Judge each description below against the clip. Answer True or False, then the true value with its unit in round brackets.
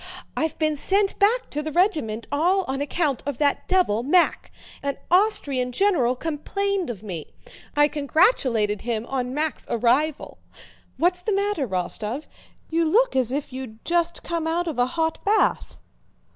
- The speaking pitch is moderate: False (300 Hz)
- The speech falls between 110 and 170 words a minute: True (155 wpm)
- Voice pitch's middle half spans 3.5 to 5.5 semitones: False (5.9 semitones)